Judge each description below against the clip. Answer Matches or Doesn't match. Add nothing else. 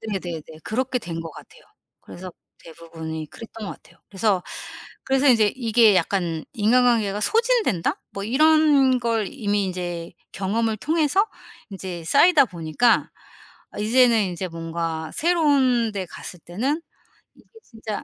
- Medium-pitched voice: Doesn't match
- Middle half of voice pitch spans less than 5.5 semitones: Doesn't match